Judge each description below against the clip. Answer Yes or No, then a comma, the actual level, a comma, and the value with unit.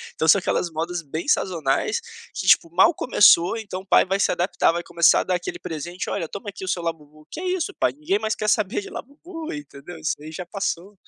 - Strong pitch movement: Yes, wide, 5.8 semitones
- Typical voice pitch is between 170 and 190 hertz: Yes, medium, 185 Hz